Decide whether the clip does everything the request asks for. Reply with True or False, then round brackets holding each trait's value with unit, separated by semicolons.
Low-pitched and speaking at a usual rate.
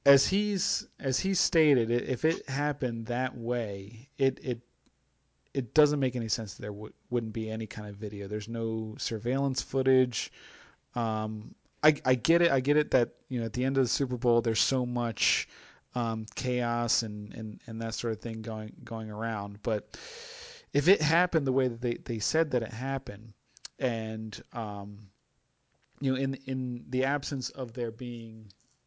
True (120 Hz; 180 wpm)